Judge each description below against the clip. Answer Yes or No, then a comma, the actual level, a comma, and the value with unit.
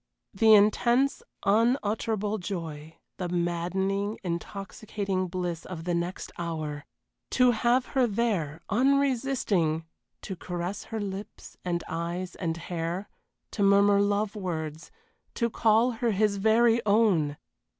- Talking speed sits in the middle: No, slow, 120 wpm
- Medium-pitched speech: No, high, 195 Hz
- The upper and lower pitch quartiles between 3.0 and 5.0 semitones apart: Yes, average, 4.3 semitones